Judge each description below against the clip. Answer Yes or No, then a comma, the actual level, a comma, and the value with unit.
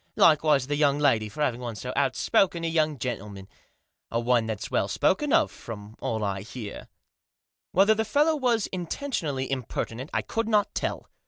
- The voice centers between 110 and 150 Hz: Yes, medium, 140 Hz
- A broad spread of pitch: Yes, wide, 7.3 semitones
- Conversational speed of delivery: Yes, average, 165 wpm